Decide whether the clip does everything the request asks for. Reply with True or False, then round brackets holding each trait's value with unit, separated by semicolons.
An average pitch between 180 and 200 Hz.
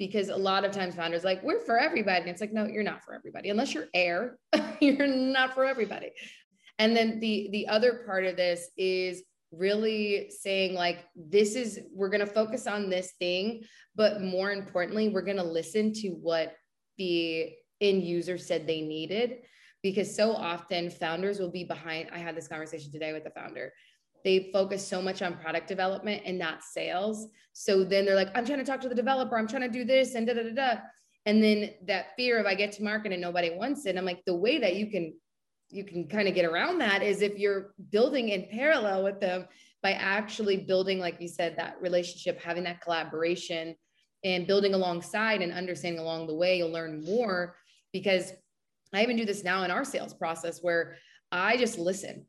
True (190 Hz)